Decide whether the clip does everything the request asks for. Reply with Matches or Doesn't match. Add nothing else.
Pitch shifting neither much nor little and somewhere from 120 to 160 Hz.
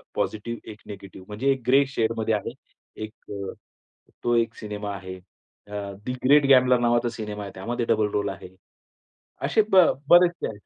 Doesn't match